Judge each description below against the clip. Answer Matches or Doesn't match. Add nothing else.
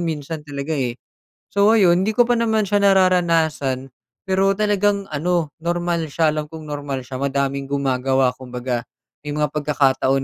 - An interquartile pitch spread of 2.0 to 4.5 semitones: Doesn't match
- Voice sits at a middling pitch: Matches